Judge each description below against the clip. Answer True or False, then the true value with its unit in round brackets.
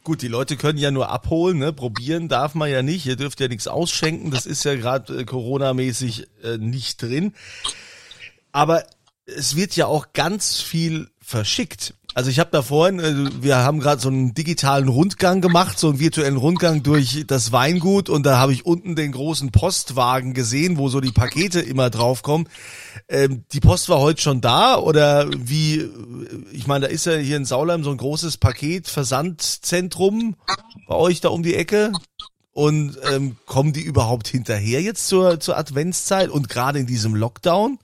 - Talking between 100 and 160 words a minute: False (180 wpm)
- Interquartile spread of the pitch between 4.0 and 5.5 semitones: True (4.3 semitones)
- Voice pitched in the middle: True (145 Hz)